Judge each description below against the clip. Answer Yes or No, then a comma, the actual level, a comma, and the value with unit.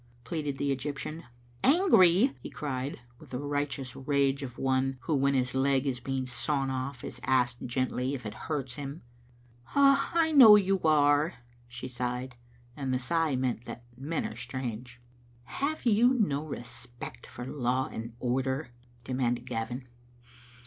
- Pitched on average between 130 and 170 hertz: Yes, low, 135 Hz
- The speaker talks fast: No, average, 155 wpm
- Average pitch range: Yes, average, 3.2 semitones